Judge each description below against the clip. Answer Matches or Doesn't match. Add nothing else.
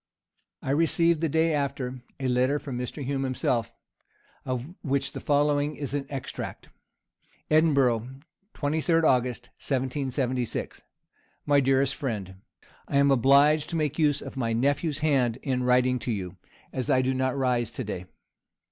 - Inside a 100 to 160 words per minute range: Matches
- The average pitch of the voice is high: Doesn't match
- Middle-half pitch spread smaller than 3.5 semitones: Matches